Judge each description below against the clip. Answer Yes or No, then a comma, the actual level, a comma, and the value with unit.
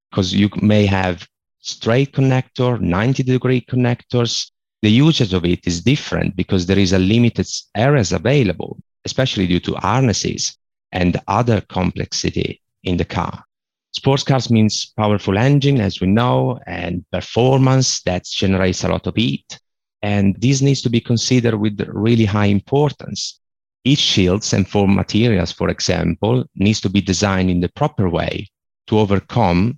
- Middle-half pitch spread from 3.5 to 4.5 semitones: No, average, 5.1 semitones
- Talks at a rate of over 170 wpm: No, average, 150 wpm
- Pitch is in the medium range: No, low, 105 Hz